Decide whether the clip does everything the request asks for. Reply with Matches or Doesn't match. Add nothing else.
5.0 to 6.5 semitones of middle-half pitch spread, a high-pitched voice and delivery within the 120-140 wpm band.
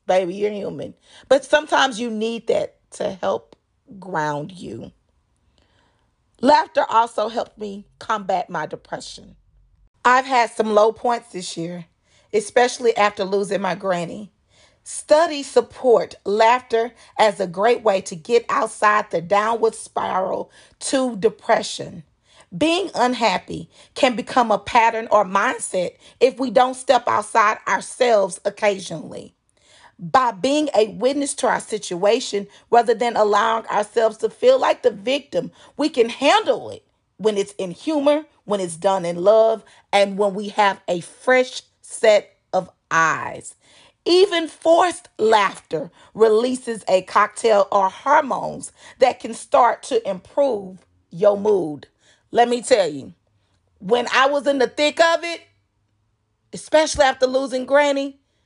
Matches